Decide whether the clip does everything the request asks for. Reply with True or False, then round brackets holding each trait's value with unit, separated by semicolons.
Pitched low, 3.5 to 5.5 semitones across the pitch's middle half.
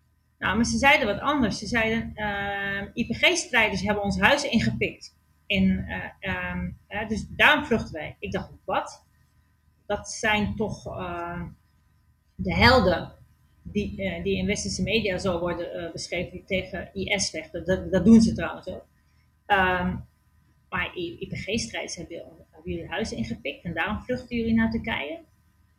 False (200 Hz; 4.1 semitones)